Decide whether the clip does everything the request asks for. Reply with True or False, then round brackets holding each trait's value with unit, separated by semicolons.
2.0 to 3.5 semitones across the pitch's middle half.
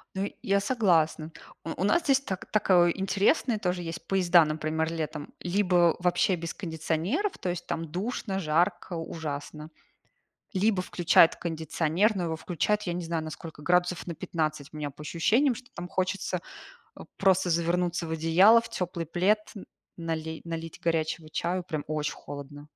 True (3.0 semitones)